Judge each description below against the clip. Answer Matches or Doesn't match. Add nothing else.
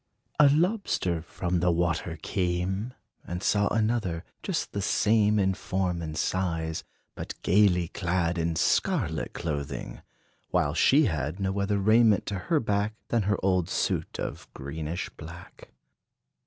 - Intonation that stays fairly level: Doesn't match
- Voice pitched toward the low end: Matches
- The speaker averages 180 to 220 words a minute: Doesn't match